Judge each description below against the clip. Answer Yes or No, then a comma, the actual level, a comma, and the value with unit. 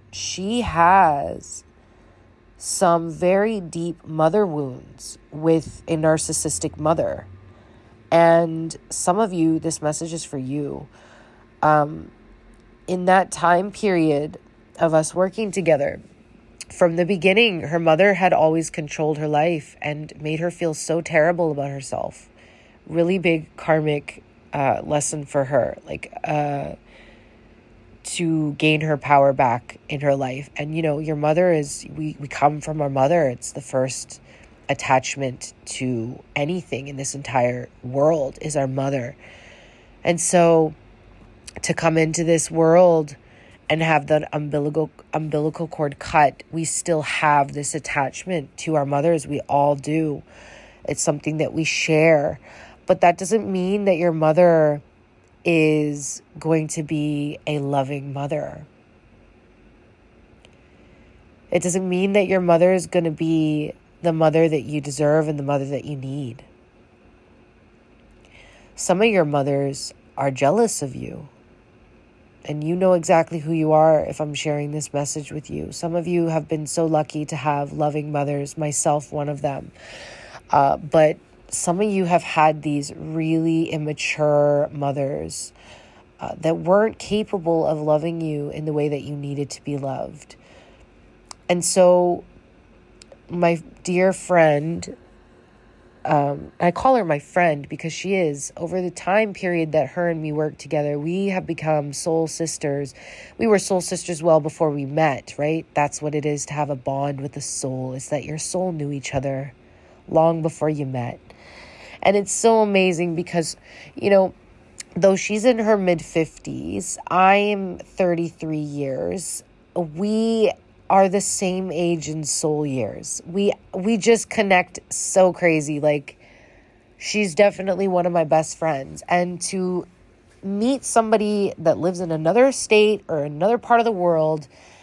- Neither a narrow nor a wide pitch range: Yes, average, 3.3 semitones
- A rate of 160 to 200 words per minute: No, average, 145 wpm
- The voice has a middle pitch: Yes, medium, 155 Hz